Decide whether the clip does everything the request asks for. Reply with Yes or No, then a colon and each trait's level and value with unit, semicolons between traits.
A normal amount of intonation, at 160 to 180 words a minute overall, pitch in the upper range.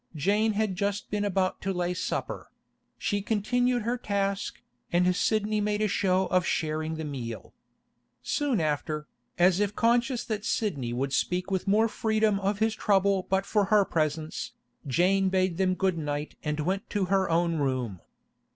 Yes: average, 4.1 semitones; average, 165 wpm; high, 195 Hz